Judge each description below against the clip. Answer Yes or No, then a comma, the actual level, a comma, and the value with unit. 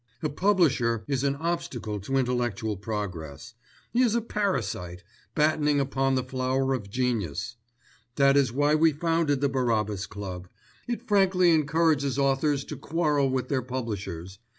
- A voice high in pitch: No, low, 135 Hz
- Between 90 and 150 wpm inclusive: Yes, average, 145 wpm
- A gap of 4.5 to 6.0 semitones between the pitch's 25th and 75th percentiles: Yes, average, 5.2 semitones